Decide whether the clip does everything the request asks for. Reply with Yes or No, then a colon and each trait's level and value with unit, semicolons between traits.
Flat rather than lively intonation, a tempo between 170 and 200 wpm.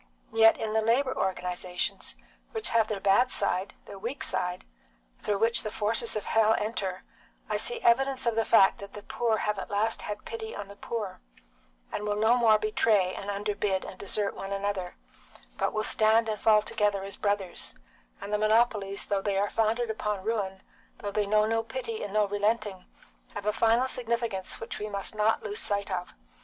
Yes: narrow, 2.1 semitones; average, 190 wpm